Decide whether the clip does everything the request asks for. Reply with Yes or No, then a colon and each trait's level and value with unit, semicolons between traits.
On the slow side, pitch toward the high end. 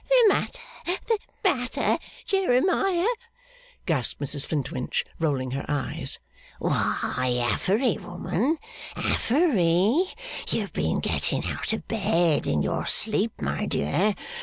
Yes: slow, 110 wpm; high, 210 Hz